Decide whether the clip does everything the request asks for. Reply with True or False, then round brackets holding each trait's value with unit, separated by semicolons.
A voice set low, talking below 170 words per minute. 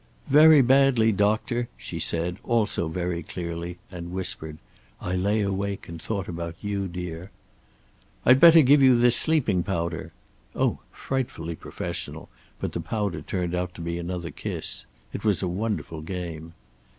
True (95 Hz; 150 wpm)